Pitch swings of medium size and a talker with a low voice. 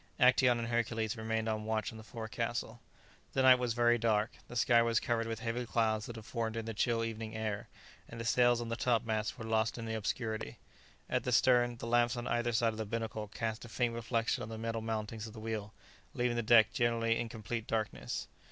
No: narrow, 1.2 semitones; low, 115 Hz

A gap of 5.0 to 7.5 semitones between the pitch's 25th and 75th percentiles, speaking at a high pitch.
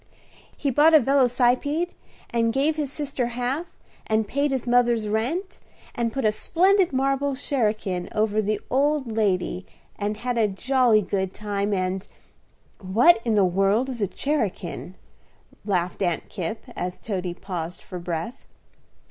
Yes: wide, 5.5 semitones; high, 225 Hz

